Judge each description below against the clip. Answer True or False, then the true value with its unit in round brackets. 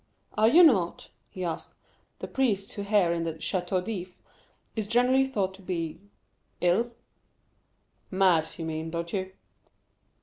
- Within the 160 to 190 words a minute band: False (135 wpm)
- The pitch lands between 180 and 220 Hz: True (190 Hz)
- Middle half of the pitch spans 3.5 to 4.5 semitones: True (4.1 semitones)